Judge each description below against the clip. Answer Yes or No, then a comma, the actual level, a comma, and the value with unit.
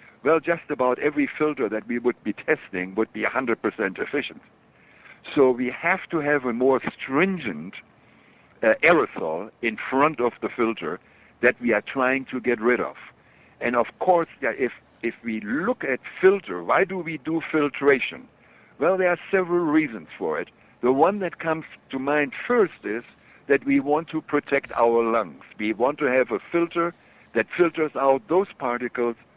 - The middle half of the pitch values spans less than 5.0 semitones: No, wide, 5.5 semitones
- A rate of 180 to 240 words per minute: No, average, 170 wpm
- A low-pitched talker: No, medium, 145 Hz